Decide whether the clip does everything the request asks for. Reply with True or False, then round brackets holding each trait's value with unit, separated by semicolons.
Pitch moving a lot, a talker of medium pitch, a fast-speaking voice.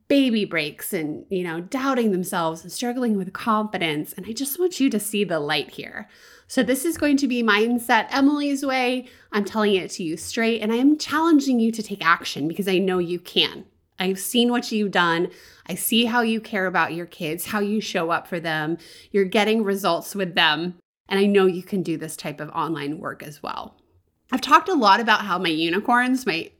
False (5.8 semitones; 200 Hz; 215 wpm)